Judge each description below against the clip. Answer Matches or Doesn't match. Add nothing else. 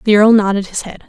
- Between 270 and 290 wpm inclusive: Matches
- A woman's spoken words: Matches